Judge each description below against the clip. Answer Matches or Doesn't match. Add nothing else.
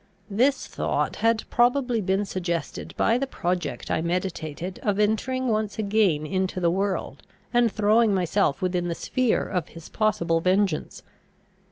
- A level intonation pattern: Doesn't match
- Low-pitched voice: Doesn't match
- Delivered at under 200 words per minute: Matches